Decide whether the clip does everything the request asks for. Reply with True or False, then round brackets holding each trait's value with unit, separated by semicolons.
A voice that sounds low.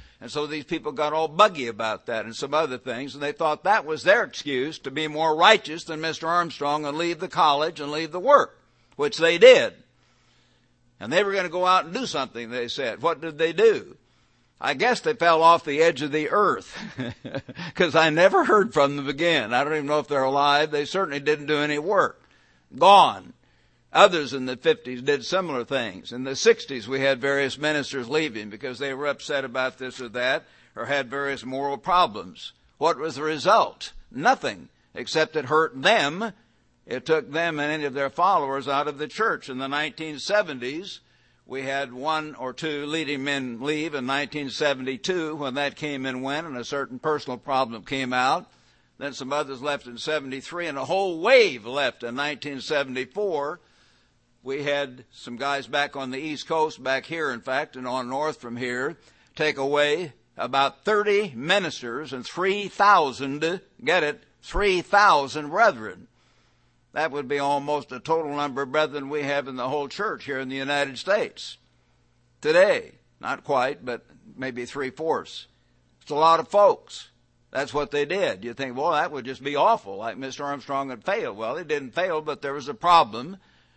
False (145 Hz)